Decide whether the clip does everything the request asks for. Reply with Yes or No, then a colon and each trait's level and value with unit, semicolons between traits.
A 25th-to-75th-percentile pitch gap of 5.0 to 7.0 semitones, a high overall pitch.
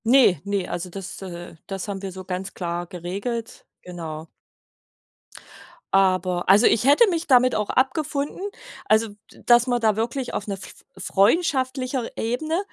Yes: wide, 5.6 semitones; high, 210 Hz